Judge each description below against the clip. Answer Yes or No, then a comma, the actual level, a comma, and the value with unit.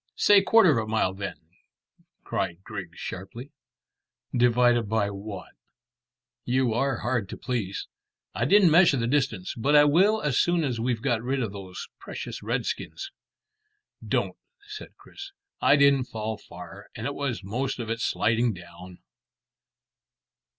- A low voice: Yes, low, 120 Hz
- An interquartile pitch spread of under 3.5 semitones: No, average, 5.2 semitones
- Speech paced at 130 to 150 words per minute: Yes, average, 145 wpm